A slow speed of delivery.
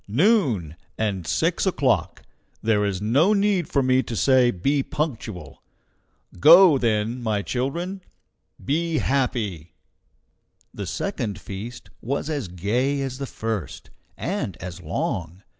Yes: slow, 125 wpm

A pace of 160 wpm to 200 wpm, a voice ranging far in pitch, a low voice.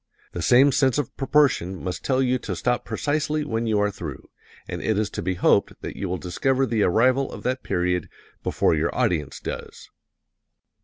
Yes: average, 190 wpm; wide, 6.6 semitones; low, 115 Hz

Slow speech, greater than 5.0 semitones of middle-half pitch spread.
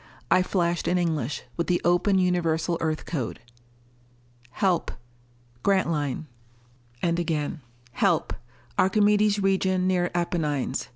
No: slow, 105 wpm; average, 2.9 semitones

